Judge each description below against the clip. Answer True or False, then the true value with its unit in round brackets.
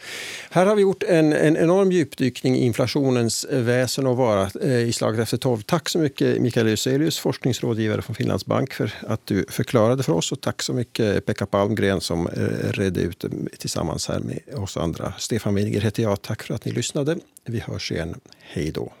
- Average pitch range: True (5.0 semitones)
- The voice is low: True (125 Hz)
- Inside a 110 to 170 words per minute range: False (190 wpm)